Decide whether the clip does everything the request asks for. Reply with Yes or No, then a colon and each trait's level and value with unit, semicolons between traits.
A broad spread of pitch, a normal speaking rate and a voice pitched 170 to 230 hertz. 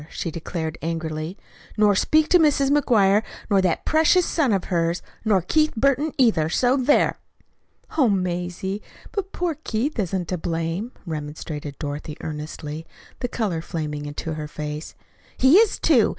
Yes: wide, 8.4 semitones; average, 150 wpm; medium, 185 Hz